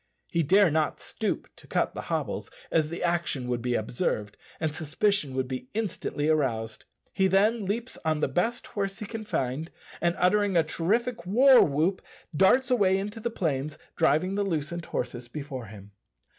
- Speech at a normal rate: Yes, average, 170 wpm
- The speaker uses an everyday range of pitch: No, wide, 6.4 semitones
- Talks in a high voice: No, medium, 170 Hz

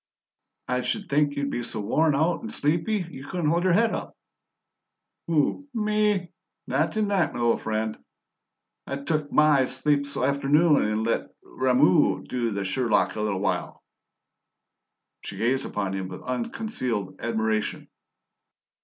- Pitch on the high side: No, medium, 140 Hz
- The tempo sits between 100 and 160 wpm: Yes, average, 140 wpm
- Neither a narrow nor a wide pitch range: No, wide, 6.4 semitones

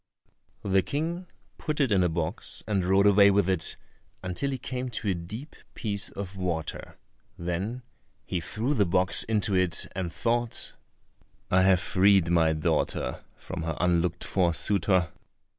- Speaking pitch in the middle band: No, very low, 95 Hz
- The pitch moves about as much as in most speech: Yes, average, 3.6 semitones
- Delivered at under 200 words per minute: Yes, average, 155 wpm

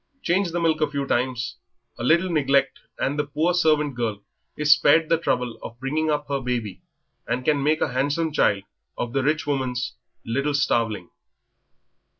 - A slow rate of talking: No, average, 170 wpm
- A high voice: No, medium, 140 Hz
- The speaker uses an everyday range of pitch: Yes, average, 3.7 semitones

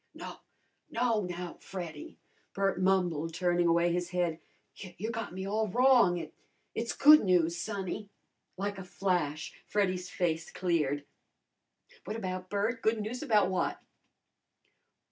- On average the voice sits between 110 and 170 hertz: No, medium, 185 Hz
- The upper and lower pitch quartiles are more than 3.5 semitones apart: No, average, 3.1 semitones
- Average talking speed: No, slow, 130 wpm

